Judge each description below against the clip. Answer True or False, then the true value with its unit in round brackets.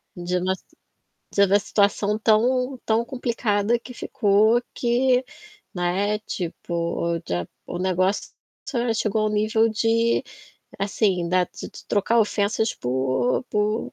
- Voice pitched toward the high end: True (210 Hz)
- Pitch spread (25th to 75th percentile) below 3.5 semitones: False (3.8 semitones)